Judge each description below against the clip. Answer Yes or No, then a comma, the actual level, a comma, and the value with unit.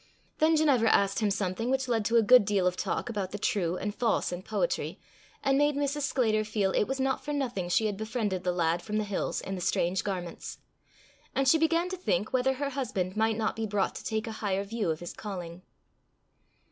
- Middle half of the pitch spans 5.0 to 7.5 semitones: Yes, average, 5.3 semitones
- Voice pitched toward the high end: Yes, high, 215 Hz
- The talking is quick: Yes, fast, 225 wpm